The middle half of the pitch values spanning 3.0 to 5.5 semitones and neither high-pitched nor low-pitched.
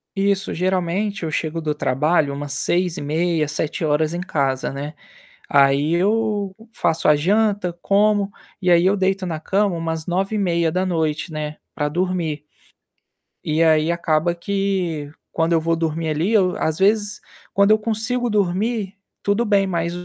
Yes: average, 4.0 semitones; medium, 175 Hz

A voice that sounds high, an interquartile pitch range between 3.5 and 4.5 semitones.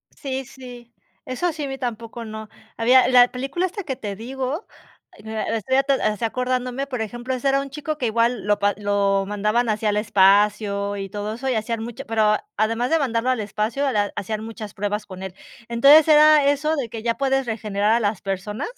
Yes: high, 230 Hz; average, 3.9 semitones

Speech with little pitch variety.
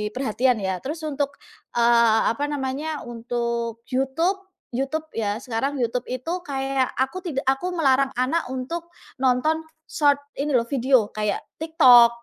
No: average, 3.6 semitones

